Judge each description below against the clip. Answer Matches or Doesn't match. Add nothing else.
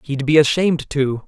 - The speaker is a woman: Doesn't match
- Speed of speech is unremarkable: Matches